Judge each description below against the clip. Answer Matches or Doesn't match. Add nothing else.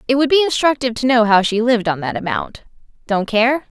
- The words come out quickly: Matches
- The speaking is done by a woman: Matches